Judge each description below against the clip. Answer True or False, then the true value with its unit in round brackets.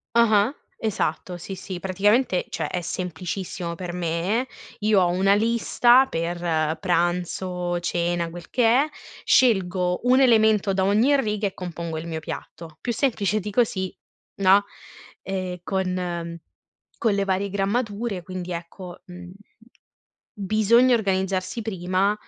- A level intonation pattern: False (3.4 semitones)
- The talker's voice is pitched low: False (190 Hz)